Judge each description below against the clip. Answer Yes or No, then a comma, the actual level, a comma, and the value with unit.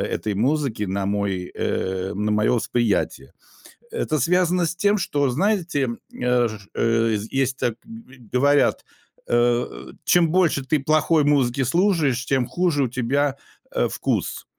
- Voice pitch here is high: No, low, 135 Hz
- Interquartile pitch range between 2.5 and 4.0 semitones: No, wide, 5.4 semitones